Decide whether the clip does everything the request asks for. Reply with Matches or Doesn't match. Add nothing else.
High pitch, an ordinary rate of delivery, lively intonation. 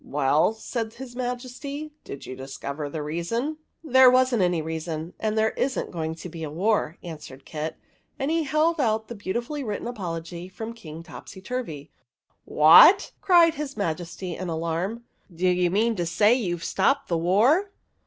Matches